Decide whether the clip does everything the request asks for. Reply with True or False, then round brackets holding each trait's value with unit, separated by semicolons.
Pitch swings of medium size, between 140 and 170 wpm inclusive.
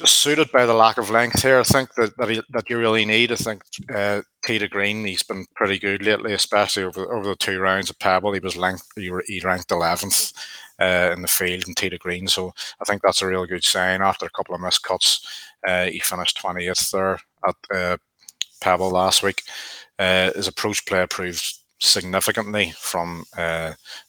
False (3.1 semitones; 195 wpm)